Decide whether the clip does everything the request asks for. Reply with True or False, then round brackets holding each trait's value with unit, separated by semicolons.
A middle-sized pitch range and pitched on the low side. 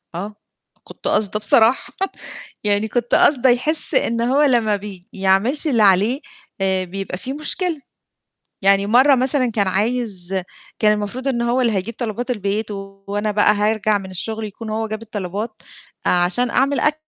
False (3.8 semitones; 215 Hz)